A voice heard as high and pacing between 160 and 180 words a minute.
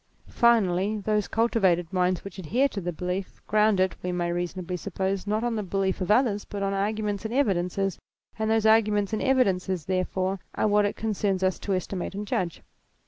No: high, 195 Hz; average, 195 wpm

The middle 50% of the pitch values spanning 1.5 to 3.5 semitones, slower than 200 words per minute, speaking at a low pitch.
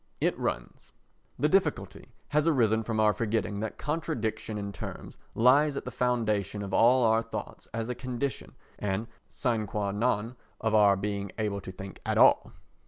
Yes: average, 3.2 semitones; average, 170 wpm; low, 110 Hz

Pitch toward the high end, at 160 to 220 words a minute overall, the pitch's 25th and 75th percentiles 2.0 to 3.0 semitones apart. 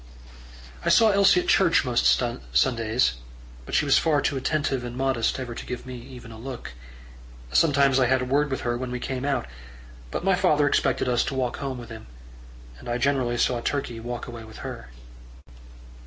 No: low, 130 Hz; average, 195 wpm; narrow, 2.6 semitones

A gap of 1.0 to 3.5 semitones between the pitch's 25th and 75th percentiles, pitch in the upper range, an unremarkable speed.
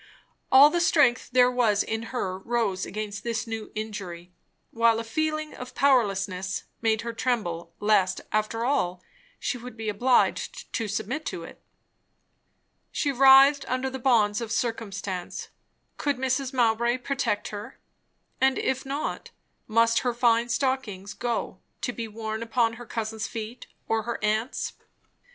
Yes: average, 3.1 semitones; high, 230 Hz; average, 145 wpm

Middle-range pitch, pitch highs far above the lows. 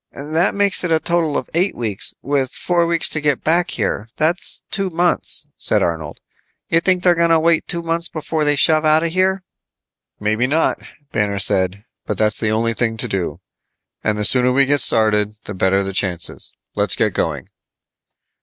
Yes: medium, 145 Hz; wide, 7.9 semitones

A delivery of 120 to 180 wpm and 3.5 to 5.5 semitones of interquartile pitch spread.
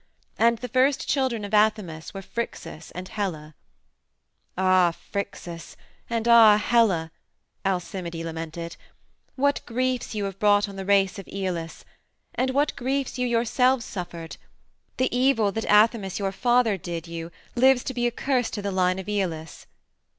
Yes: average, 150 wpm; average, 4.9 semitones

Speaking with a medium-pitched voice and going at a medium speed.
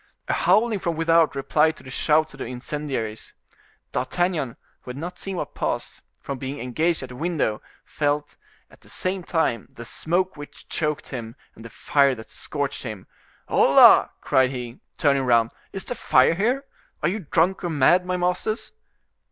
Yes: medium, 150 Hz; average, 175 wpm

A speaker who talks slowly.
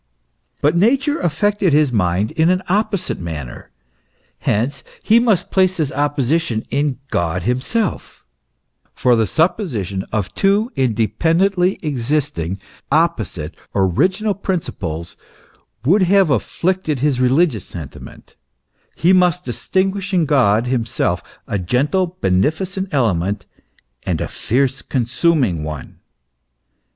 Yes: slow, 110 wpm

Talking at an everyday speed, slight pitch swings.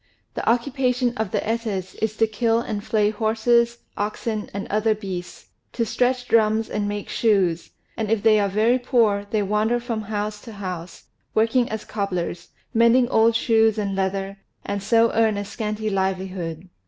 Yes: average, 165 wpm; narrow, 2.3 semitones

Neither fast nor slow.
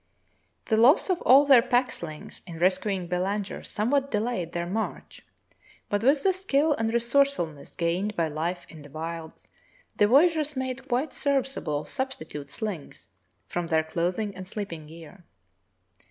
Yes: average, 150 wpm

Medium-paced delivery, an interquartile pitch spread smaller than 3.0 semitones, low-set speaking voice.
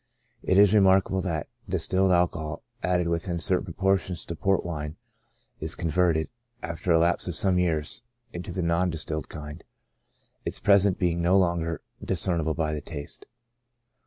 Yes: average, 155 wpm; narrow, 2.4 semitones; very low, 85 Hz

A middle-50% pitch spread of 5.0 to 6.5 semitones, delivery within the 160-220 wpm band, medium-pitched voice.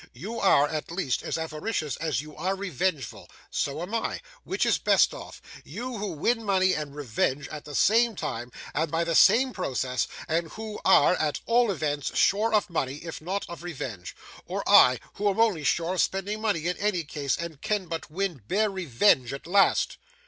Yes: average, 5.3 semitones; average, 190 wpm; medium, 170 Hz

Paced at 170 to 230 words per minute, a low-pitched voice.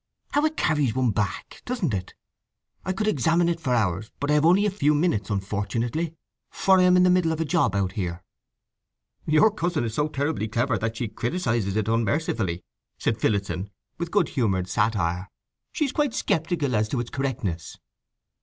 Yes: average, 185 wpm; low, 130 Hz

